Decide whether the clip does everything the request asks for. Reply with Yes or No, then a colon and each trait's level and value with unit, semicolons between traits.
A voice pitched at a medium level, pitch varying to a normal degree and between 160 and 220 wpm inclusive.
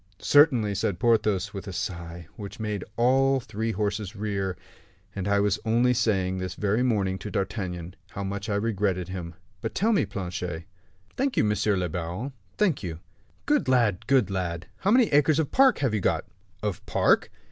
No: low, 105 Hz; average, 4.2 semitones; average, 180 wpm